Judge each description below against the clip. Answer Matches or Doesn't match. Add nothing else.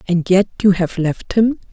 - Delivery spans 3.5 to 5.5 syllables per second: Matches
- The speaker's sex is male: Doesn't match